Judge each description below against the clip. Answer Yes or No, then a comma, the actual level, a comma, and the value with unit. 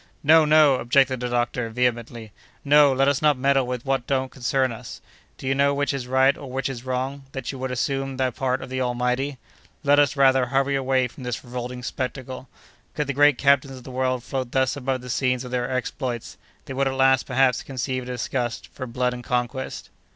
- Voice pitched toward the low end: Yes, low, 130 Hz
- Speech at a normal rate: No, fast, 210 wpm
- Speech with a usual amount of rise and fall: No, narrow, 1.5 semitones